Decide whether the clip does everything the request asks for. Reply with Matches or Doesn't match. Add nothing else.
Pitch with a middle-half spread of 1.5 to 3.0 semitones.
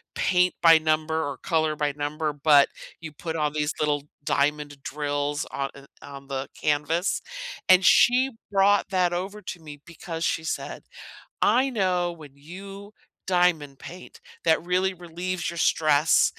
Doesn't match